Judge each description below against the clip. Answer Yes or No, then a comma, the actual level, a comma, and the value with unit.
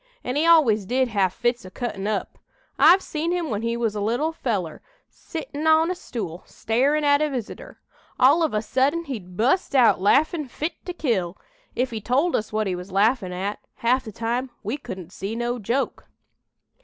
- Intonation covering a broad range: Yes, wide, 5.8 semitones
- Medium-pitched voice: No, high, 240 Hz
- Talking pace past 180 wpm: Yes, average, 190 wpm